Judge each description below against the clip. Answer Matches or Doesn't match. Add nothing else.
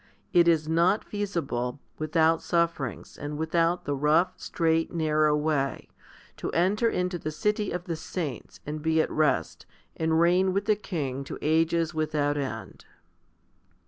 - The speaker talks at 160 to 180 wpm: Doesn't match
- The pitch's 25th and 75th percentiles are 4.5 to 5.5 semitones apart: Doesn't match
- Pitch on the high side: Doesn't match